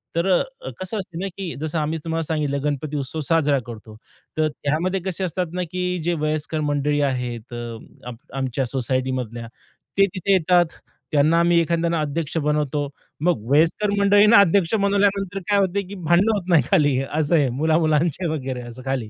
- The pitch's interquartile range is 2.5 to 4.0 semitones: No, average, 4.4 semitones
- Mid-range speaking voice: Yes, medium, 160 Hz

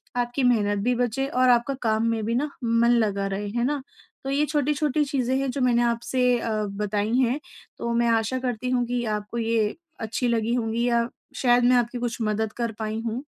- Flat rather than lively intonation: Yes, narrow, 2.2 semitones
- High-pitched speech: Yes, high, 240 Hz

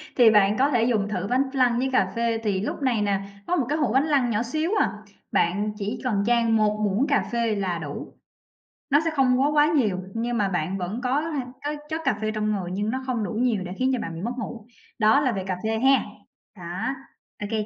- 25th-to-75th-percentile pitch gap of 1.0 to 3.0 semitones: No, average, 4.2 semitones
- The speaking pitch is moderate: No, high, 230 Hz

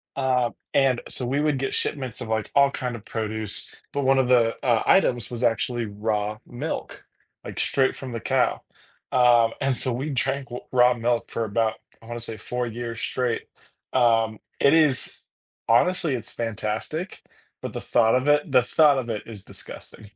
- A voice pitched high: No, low, 120 Hz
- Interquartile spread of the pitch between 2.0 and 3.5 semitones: Yes, average, 2.8 semitones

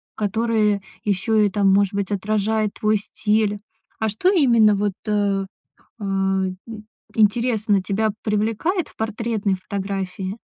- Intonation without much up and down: Yes, narrow, 1.8 semitones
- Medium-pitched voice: No, high, 210 Hz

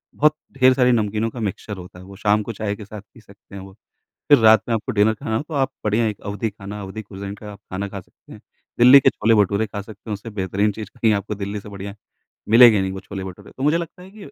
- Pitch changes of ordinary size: No, narrow, 2.3 semitones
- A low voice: Yes, low, 105 Hz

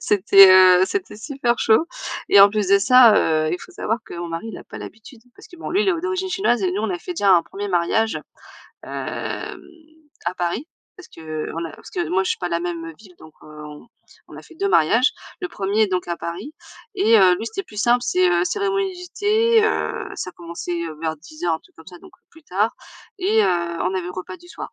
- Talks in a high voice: Yes, high, 200 Hz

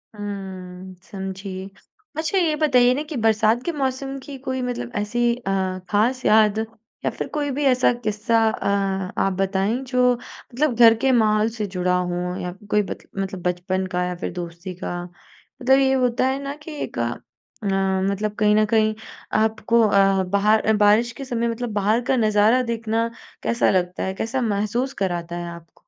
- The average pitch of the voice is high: Yes, high, 215 Hz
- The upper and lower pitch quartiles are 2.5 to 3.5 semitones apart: No, average, 4.3 semitones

